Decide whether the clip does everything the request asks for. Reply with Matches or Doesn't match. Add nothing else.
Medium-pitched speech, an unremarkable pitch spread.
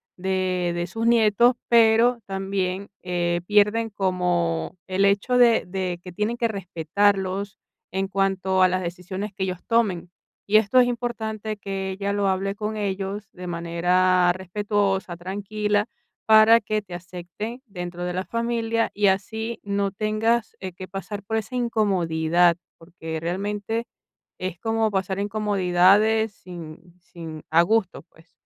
Doesn't match